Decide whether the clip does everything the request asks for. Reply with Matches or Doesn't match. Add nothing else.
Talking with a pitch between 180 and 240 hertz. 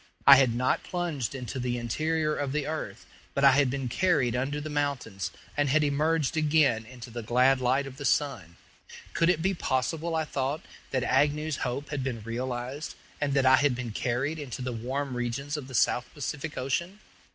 Doesn't match